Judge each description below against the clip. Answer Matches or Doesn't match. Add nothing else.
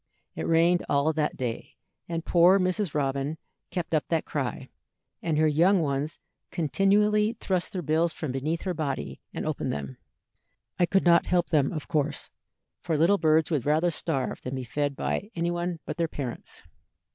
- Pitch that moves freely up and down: Doesn't match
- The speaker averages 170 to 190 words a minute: Matches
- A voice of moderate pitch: Matches